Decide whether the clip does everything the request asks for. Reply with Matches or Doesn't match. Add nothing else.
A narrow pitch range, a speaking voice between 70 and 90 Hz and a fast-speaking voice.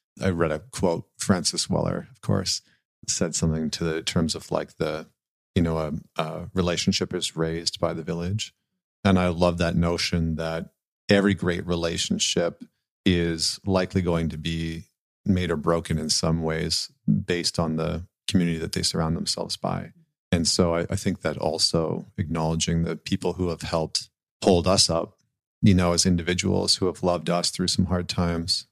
Doesn't match